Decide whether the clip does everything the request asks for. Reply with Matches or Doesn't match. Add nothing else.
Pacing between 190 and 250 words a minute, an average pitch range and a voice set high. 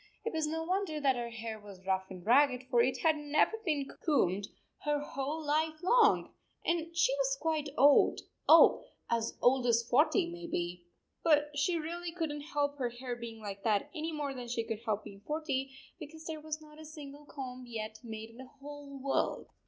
Matches